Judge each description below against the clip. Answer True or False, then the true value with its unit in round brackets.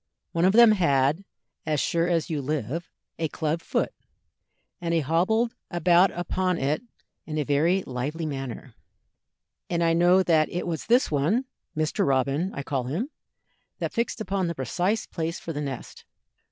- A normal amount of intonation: True (3.8 semitones)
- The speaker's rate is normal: True (165 wpm)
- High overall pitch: False (165 Hz)